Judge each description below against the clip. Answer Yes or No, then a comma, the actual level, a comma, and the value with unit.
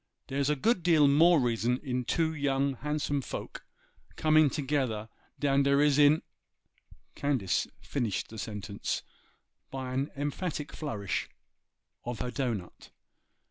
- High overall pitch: No, medium, 140 Hz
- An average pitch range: Yes, average, 3.2 semitones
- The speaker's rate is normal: No, slow, 130 wpm